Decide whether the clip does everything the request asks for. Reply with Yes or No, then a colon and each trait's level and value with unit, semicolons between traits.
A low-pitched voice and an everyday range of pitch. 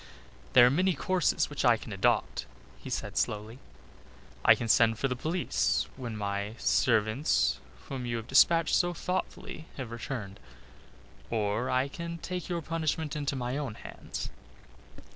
No: low, 130 Hz; wide, 6.2 semitones